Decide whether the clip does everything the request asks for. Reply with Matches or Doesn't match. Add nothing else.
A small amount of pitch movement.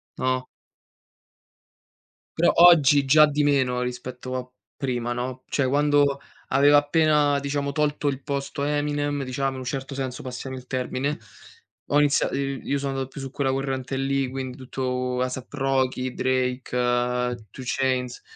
Matches